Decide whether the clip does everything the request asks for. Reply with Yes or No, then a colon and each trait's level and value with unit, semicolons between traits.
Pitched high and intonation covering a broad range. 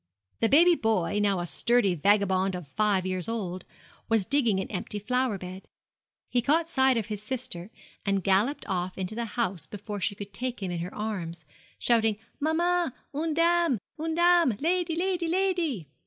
Yes: high, 220 Hz; wide, 7.7 semitones